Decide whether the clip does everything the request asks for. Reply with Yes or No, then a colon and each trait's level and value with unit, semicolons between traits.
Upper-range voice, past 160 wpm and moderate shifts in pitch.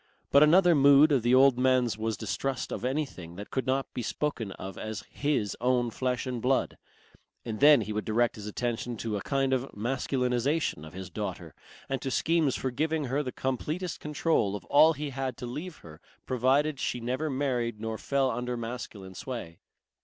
No: low, 125 Hz; average, 190 wpm; average, 3.7 semitones